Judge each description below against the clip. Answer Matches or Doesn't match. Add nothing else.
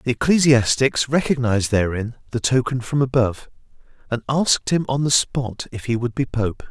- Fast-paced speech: Doesn't match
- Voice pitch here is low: Matches